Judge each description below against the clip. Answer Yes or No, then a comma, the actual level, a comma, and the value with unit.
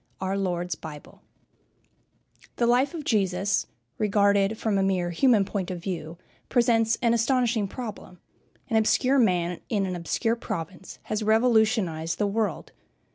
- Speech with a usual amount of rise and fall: Yes, average, 4.0 semitones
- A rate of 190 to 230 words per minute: No, average, 140 wpm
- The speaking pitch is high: Yes, high, 205 Hz